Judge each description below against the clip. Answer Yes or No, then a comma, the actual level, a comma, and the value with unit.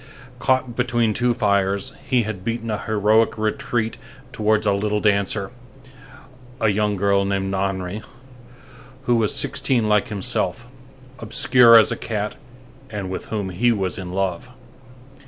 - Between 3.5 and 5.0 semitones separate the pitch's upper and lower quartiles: No, average, 2.7 semitones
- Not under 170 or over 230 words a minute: No, average, 140 wpm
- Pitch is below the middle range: Yes, low, 105 Hz